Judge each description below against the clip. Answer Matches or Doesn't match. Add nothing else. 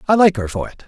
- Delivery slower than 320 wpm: Doesn't match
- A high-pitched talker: Doesn't match